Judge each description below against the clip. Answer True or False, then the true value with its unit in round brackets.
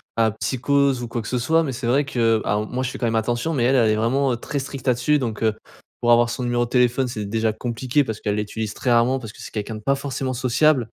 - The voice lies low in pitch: True (120 Hz)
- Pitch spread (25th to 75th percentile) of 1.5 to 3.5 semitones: True (2.8 semitones)